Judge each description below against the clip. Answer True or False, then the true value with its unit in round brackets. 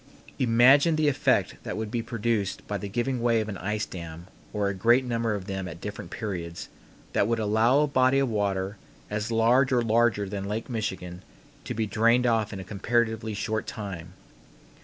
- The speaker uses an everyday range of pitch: True (3.0 semitones)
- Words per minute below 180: False (190 wpm)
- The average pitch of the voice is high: False (110 Hz)